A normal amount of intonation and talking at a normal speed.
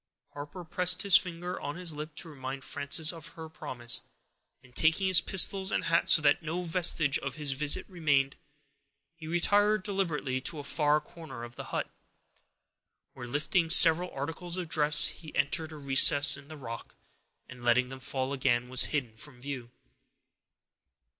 Yes: average, 3.9 semitones; average, 165 wpm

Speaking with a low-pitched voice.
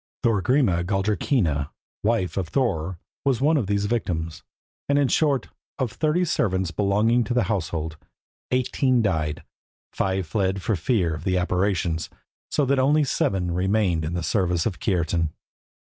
Yes: very low, 95 Hz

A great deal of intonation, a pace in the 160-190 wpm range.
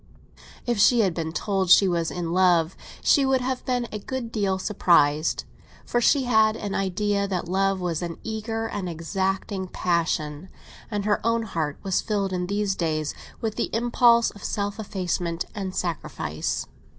No: average, 4.0 semitones; average, 165 wpm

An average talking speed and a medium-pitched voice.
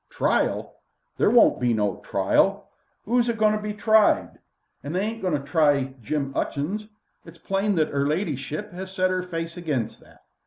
Yes: average, 170 wpm; medium, 175 Hz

